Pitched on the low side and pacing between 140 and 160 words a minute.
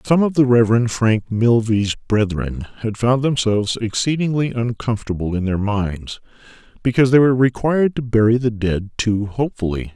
Yes: low, 115 Hz; average, 150 wpm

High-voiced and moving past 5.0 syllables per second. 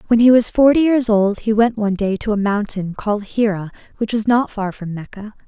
Yes: high, 215 Hz; 5.5 syllables/s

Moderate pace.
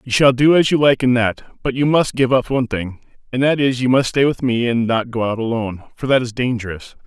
No: fast, 270 wpm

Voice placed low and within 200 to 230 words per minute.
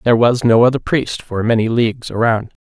Yes: low, 115 Hz; fast, 205 wpm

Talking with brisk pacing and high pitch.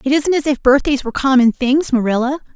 Yes: fast, 210 wpm; very high, 270 Hz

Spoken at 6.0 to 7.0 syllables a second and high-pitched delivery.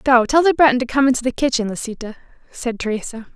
Yes: 6.7 syllables/s; very high, 250 Hz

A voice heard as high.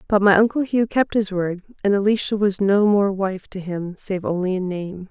Yes: high, 195 Hz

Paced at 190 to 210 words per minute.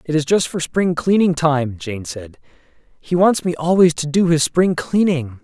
Yes: average, 200 wpm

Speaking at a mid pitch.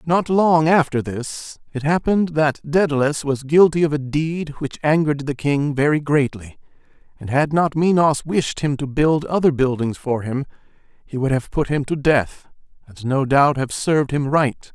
Yes: medium, 145 Hz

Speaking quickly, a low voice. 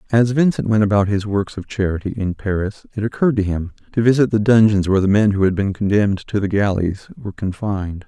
Yes: fast, 225 wpm; low, 100 Hz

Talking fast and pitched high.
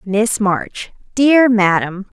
No: slow, 110 wpm; high, 215 Hz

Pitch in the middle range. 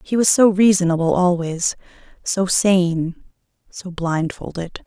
Yes: medium, 180 Hz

